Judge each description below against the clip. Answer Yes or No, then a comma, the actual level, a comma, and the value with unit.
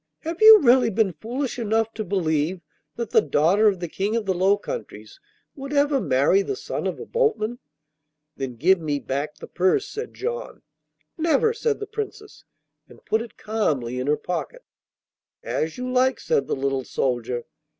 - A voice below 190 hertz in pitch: No, high, 215 Hz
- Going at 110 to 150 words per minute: No, average, 175 wpm